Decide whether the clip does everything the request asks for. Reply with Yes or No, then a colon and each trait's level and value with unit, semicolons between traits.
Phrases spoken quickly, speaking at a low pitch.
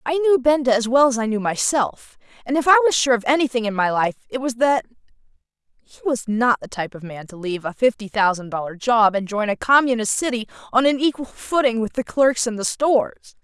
No: fast, 230 wpm; high, 240 Hz